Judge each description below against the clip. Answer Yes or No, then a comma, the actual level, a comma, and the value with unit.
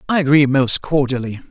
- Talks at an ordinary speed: Yes, average, 160 wpm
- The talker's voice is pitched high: No, low, 135 Hz